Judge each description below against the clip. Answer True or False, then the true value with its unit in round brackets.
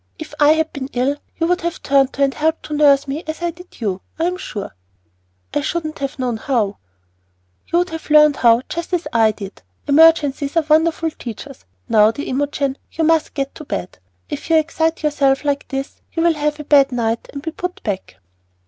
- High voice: True (290 Hz)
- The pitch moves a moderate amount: True (3.2 semitones)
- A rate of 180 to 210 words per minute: True (205 wpm)